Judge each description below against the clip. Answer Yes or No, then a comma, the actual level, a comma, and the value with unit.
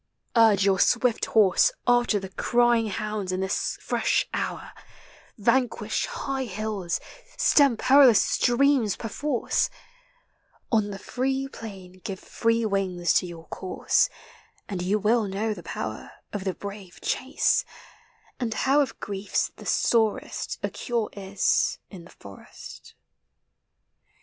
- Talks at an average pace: No, slow, 130 wpm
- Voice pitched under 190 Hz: No, high, 215 Hz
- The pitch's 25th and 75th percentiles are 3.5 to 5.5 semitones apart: Yes, average, 3.9 semitones